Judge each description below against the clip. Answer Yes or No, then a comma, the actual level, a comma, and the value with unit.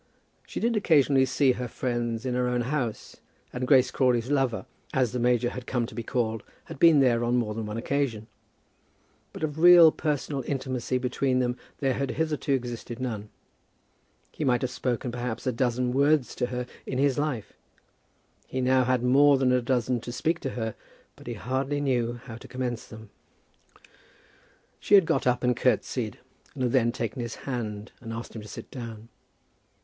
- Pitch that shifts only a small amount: Yes, narrow, 2.3 semitones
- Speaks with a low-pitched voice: Yes, low, 125 Hz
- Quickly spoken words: No, average, 185 wpm